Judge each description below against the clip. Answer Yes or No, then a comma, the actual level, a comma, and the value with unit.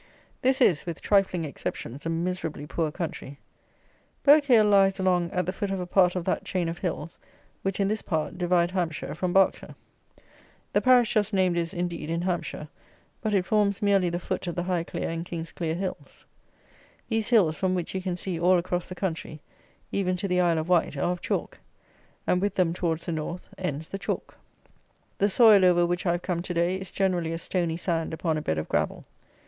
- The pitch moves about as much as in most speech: No, narrow, 2.3 semitones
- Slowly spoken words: No, average, 200 wpm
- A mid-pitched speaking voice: Yes, medium, 180 Hz